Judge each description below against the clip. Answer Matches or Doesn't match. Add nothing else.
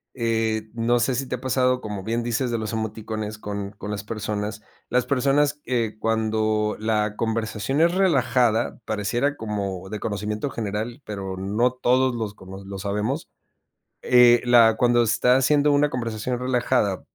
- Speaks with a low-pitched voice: Matches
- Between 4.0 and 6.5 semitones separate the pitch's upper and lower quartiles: Doesn't match